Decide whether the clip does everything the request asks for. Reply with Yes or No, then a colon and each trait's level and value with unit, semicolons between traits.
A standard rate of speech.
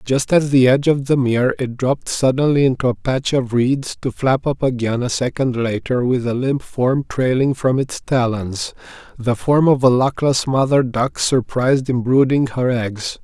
Yes: average, 185 wpm